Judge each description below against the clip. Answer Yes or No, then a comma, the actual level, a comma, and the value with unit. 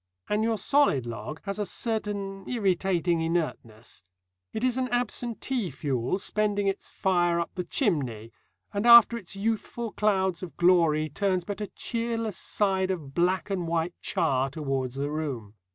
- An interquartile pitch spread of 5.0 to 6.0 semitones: Yes, wide, 5.4 semitones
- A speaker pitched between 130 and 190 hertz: Yes, medium, 185 Hz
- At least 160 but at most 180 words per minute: No, average, 150 wpm